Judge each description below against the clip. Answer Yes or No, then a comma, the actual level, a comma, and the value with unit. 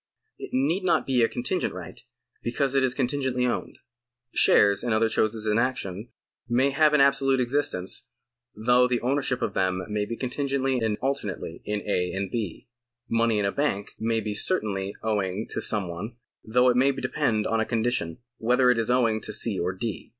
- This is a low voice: Yes, low, 115 Hz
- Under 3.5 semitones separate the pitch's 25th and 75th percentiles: No, average, 3.9 semitones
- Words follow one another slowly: No, average, 185 wpm